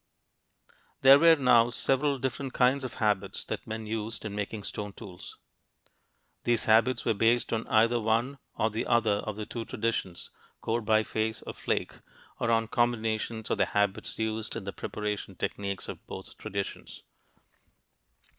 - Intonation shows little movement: Yes, narrow, 2.1 semitones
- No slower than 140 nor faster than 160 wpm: Yes, average, 155 wpm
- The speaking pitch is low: Yes, low, 110 Hz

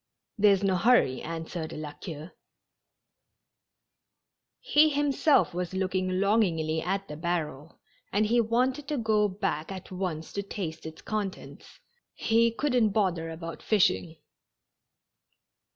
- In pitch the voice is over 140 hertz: Yes, high, 190 Hz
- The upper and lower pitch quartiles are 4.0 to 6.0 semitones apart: Yes, average, 5.1 semitones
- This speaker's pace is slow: Yes, slow, 120 wpm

